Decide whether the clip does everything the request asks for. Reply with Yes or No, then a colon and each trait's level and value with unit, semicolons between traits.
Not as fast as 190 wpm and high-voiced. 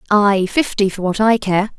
No: average, 200 wpm; high, 205 Hz